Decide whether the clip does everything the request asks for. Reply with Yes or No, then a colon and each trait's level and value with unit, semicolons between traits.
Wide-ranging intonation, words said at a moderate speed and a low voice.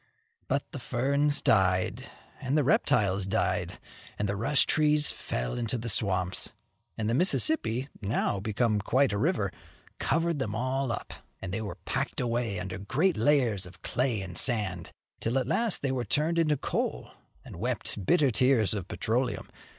Yes: wide, 5.7 semitones; average, 160 wpm; low, 115 Hz